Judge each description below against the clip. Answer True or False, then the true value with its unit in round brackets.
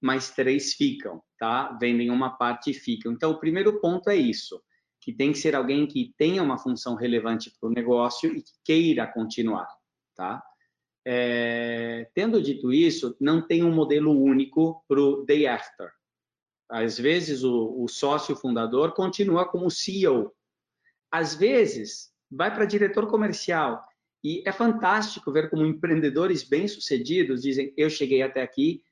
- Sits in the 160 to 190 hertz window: False (145 Hz)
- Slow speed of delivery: False (155 wpm)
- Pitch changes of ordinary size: False (7.1 semitones)